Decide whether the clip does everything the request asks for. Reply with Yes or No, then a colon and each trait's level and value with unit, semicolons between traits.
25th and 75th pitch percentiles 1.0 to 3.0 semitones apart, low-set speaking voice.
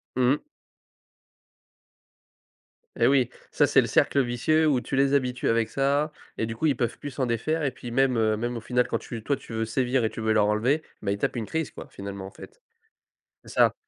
No: average, 3.6 semitones; low, 125 Hz